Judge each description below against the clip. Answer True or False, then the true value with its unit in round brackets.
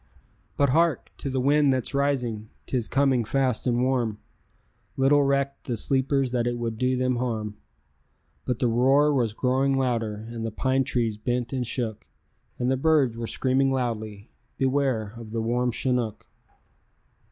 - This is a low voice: True (125 Hz)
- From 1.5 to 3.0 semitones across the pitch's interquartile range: True (2.7 semitones)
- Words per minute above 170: False (160 wpm)